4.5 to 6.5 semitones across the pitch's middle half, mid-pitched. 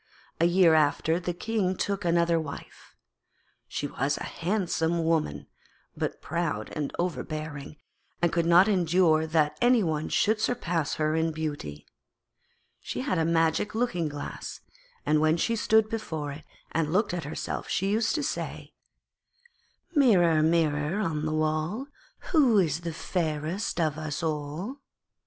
No: average, 3.3 semitones; medium, 165 Hz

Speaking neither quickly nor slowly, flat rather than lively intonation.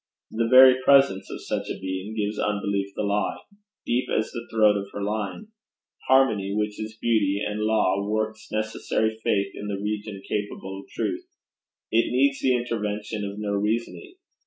Yes: average, 165 wpm; narrow, 2.1 semitones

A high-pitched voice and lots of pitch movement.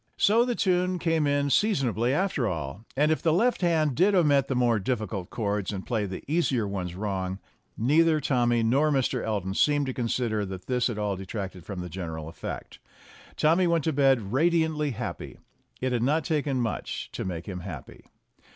No: low, 125 Hz; wide, 7.5 semitones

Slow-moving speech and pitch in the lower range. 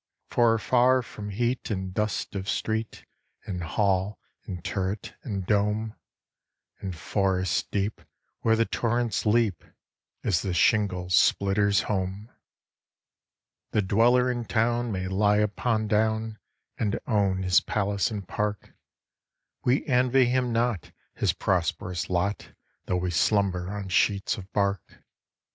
Yes: slow, 125 wpm; low, 105 Hz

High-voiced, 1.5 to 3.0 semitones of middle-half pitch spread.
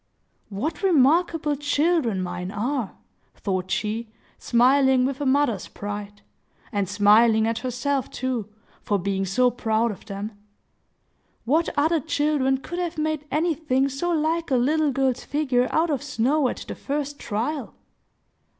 No: very high, 260 Hz; average, 5.3 semitones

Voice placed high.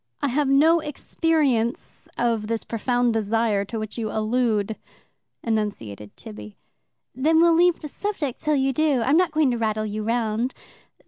Yes: high, 240 Hz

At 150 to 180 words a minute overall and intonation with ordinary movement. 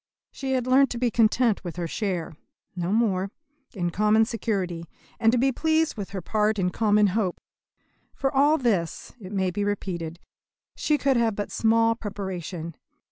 Yes: average, 175 wpm; average, 4.3 semitones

